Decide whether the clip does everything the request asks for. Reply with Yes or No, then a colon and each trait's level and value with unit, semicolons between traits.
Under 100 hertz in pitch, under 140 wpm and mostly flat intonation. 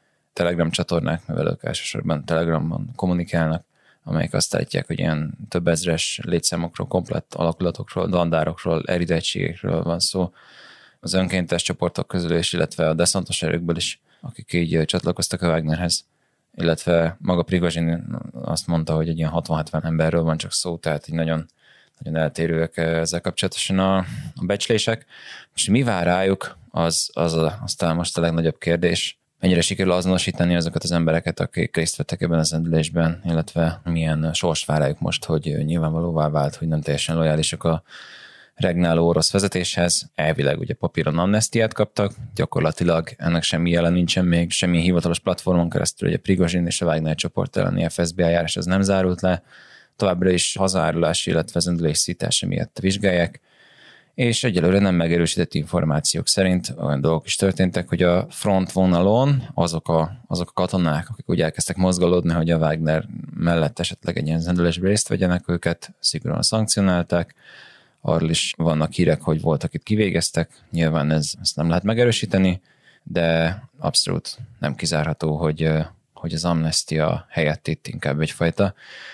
No: very low, 85 Hz; average, 150 wpm; narrow, 2.1 semitones